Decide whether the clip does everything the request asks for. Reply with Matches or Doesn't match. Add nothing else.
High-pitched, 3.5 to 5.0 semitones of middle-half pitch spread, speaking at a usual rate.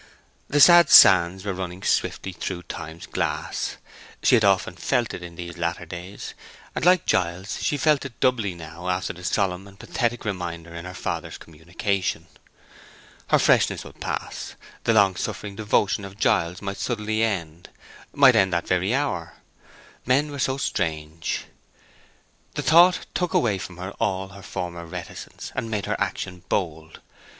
Doesn't match